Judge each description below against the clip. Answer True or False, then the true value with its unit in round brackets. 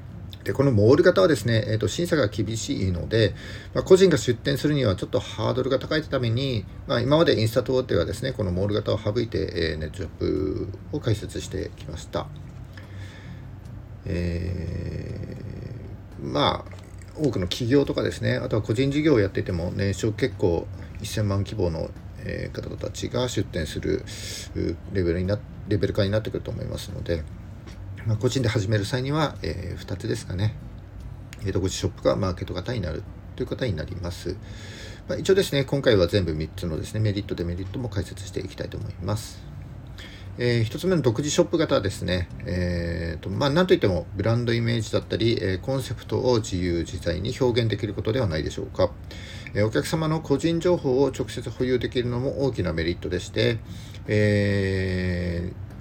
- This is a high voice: False (105 Hz)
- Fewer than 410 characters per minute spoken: True (370 characters per minute)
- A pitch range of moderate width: True (4.6 semitones)